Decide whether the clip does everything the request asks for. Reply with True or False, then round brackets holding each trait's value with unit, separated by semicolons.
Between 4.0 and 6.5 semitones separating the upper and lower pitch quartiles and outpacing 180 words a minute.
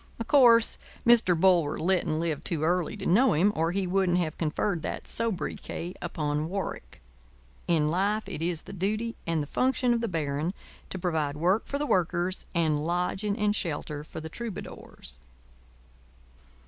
False (4.5 semitones; 160 wpm)